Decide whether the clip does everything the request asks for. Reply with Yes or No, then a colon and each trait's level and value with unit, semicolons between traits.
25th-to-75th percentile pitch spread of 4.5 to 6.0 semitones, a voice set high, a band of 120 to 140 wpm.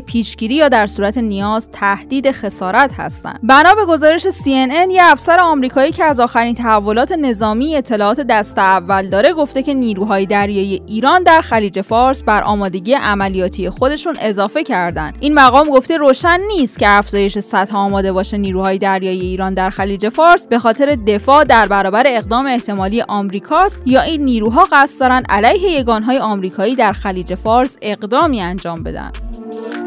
No: wide, 5.6 semitones; high, 230 Hz; fast, 155 wpm